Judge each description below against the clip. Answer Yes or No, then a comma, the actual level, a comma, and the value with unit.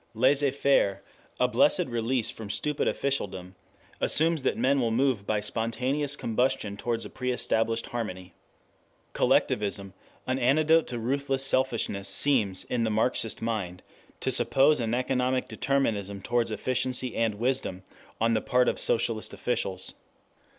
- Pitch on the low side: Yes, low, 120 Hz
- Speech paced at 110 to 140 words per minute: Yes, slow, 135 wpm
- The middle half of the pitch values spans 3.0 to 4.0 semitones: Yes, average, 3.6 semitones